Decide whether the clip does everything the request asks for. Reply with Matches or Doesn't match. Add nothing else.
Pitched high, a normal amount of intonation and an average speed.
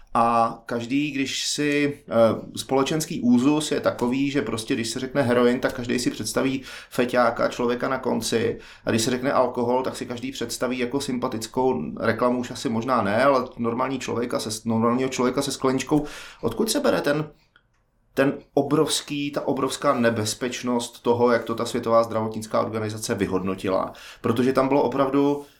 Doesn't match